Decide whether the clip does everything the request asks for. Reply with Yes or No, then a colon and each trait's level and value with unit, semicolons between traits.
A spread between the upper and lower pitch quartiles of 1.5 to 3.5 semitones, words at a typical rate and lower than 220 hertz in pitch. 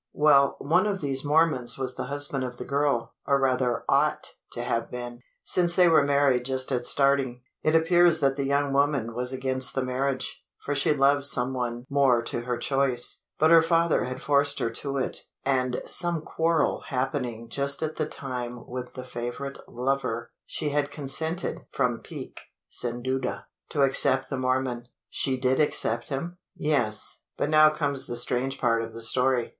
Yes: narrow, 2.6 semitones; average, 180 wpm; low, 135 Hz